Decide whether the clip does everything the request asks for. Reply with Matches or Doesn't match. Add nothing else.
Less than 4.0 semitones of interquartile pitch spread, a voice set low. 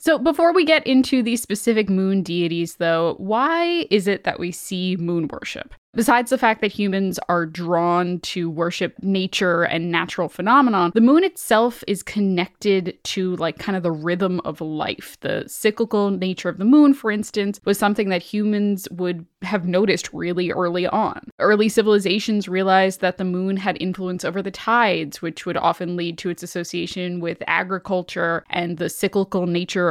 Doesn't match